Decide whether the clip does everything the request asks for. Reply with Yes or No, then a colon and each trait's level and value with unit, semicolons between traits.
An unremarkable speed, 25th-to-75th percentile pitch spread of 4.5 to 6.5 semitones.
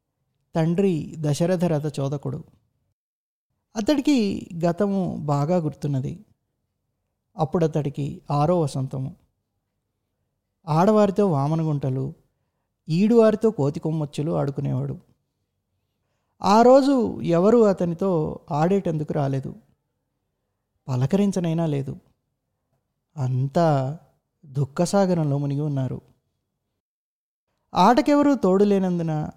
No: slow, 65 wpm; average, 5.3 semitones